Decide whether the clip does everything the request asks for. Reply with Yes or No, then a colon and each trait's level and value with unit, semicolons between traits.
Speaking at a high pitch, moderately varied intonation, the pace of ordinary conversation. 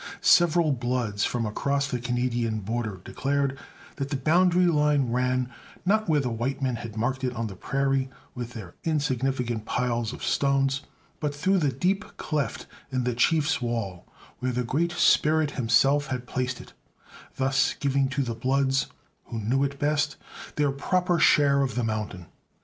No: low, 135 Hz; average, 3.1 semitones; average, 165 wpm